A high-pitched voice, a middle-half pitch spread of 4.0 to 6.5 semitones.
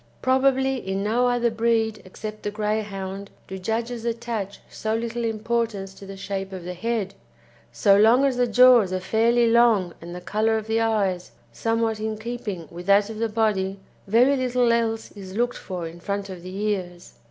No: high, 215 Hz; average, 3.3 semitones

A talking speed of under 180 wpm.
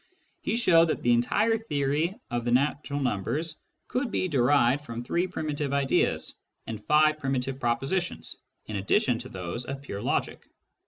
Yes: average, 155 wpm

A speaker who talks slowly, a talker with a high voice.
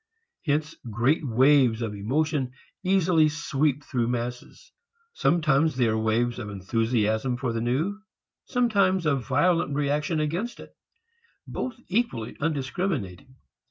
No: slow, 120 wpm; medium, 140 Hz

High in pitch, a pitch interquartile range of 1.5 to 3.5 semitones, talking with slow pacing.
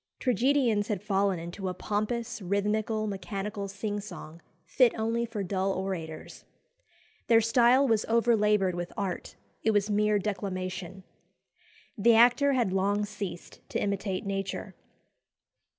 Yes: high, 205 Hz; average, 2.7 semitones; slow, 125 wpm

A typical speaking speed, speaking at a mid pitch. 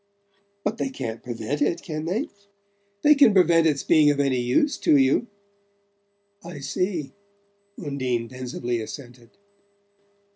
No: slow, 125 wpm; medium, 145 Hz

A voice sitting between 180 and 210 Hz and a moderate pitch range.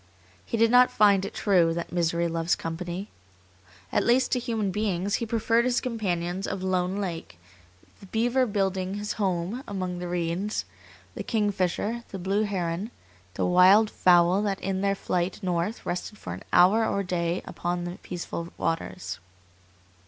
Yes: high, 190 Hz; average, 3.2 semitones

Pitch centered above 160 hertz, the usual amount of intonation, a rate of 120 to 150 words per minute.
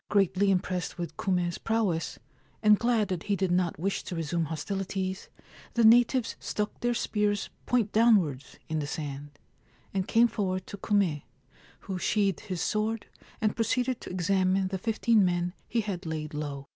No: high, 190 Hz; average, 3.6 semitones; average, 160 wpm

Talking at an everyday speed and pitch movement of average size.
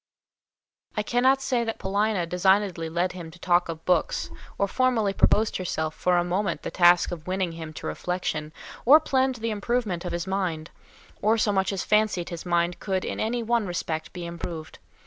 Yes: average, 190 wpm; average, 3.9 semitones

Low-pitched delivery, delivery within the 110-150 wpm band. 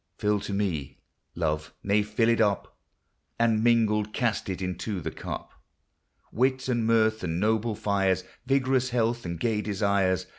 Yes: low, 105 Hz; average, 145 wpm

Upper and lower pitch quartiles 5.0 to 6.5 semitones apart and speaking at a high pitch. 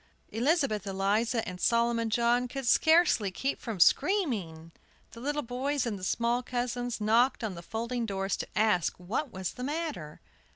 No: average, 4.2 semitones; high, 235 Hz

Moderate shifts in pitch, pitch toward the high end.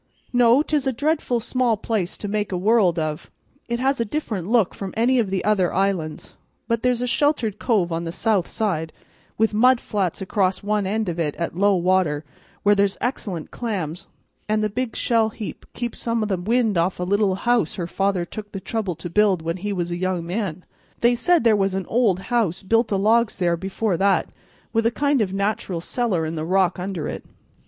Yes: average, 4.2 semitones; high, 205 Hz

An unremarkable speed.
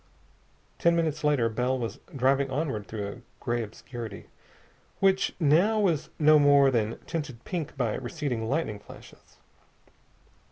No: slow, 130 wpm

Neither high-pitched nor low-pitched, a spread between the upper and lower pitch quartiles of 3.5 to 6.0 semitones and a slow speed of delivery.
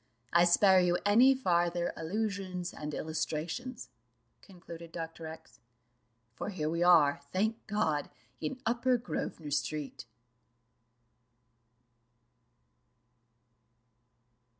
Yes: medium, 175 Hz; average, 4.4 semitones; slow, 85 wpm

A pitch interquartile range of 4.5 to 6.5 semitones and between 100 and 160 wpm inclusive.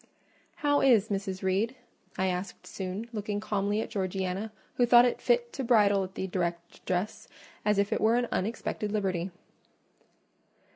No: average, 3.2 semitones; average, 150 wpm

